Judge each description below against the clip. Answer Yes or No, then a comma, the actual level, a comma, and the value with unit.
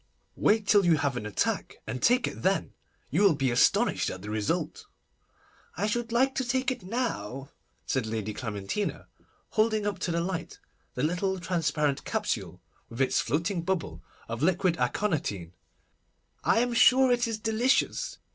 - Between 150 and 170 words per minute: Yes, average, 160 wpm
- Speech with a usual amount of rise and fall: No, wide, 9.0 semitones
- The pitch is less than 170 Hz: No, medium, 180 Hz